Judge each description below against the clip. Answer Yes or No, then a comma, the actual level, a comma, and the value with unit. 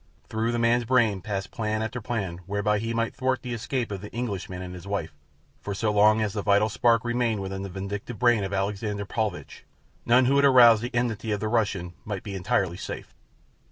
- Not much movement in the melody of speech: No, average, 3.1 semitones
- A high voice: No, low, 110 Hz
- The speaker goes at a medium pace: No, fast, 210 wpm